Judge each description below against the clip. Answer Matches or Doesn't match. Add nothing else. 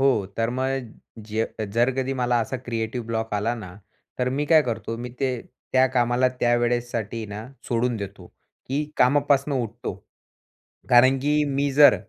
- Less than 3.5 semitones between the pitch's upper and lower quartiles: Matches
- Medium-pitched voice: Doesn't match